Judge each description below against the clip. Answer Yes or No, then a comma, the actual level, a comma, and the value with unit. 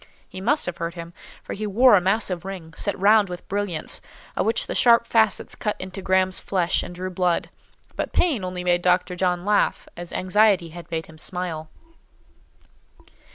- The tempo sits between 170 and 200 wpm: Yes, average, 180 wpm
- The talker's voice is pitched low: No, medium, 185 Hz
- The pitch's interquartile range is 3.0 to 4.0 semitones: No, narrow, 2.6 semitones